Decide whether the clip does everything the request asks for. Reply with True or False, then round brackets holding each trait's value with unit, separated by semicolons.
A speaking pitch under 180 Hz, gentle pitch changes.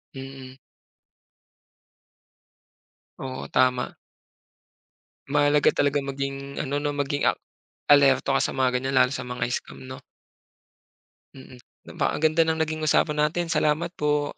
True (140 Hz; 2.2 semitones)